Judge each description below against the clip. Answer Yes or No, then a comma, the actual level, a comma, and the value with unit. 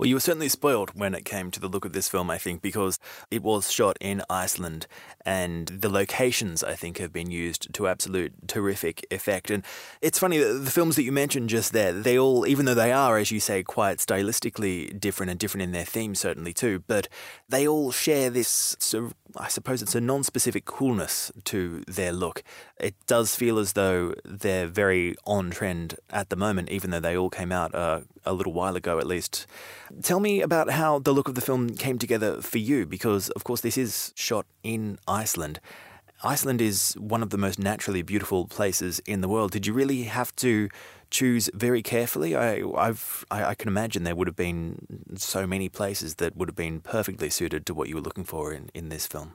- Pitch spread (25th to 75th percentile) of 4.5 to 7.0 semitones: Yes, average, 4.9 semitones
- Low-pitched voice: Yes, low, 105 Hz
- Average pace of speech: No, fast, 210 wpm